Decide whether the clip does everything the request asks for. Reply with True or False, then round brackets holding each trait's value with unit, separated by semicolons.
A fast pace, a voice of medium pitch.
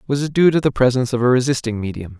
False (275 wpm; 130 Hz)